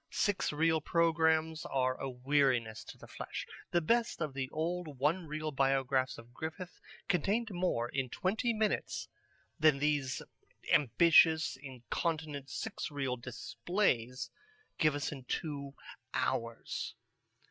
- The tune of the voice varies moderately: Yes, average, 3.8 semitones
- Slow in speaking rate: Yes, slow, 125 wpm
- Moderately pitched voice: Yes, medium, 150 Hz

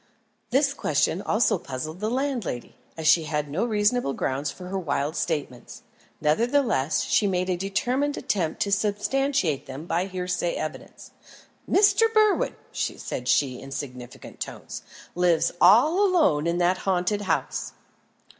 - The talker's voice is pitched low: No, medium, 185 Hz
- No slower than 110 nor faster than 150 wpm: Yes, slow, 135 wpm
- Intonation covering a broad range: Yes, wide, 7.3 semitones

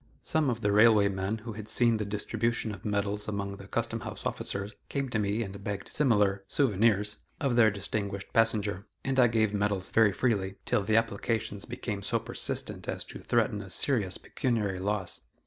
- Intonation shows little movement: Yes, narrow, 2.3 semitones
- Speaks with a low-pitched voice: Yes, low, 105 Hz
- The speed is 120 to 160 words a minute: No, average, 185 wpm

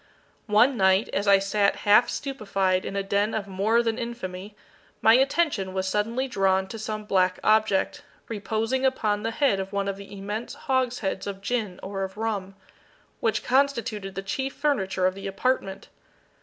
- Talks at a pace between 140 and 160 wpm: No, average, 170 wpm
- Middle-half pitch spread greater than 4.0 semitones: No, average, 3.2 semitones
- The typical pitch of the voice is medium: No, high, 205 Hz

